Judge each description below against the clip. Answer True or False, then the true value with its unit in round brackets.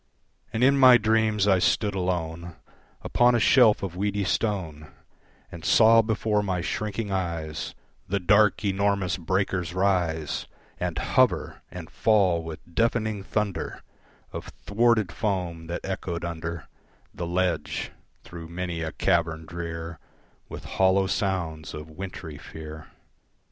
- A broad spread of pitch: False (3.8 semitones)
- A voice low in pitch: True (95 Hz)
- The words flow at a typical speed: False (130 wpm)